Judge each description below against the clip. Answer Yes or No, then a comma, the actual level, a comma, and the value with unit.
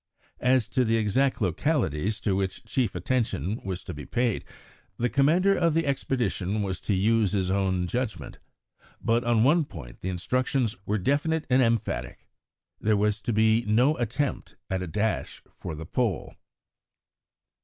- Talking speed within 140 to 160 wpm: Yes, average, 155 wpm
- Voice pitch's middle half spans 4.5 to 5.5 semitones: Yes, average, 5.1 semitones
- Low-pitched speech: Yes, low, 110 Hz